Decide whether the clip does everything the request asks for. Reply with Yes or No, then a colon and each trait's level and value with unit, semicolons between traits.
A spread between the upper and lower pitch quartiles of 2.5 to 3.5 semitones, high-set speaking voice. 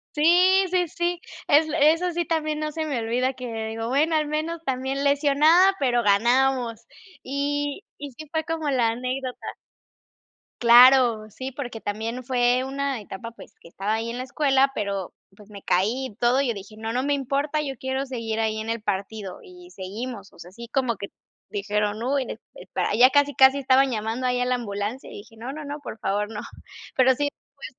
No: average, 4.3 semitones; very high, 255 Hz